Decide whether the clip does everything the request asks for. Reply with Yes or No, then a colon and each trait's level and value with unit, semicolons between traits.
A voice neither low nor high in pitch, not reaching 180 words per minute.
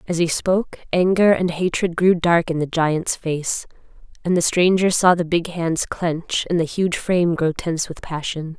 No: medium, 170 Hz; average, 195 wpm